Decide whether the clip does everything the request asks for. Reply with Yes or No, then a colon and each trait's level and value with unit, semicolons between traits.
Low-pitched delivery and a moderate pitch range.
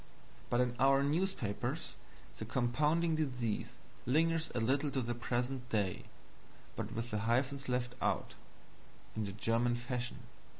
Yes: low, 125 Hz; average, 3.0 semitones